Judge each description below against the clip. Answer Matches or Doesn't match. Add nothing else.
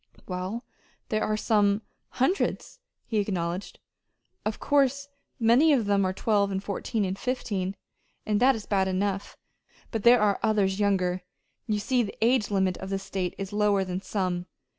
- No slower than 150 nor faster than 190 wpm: Matches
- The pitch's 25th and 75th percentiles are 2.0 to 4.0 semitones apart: Matches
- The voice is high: Matches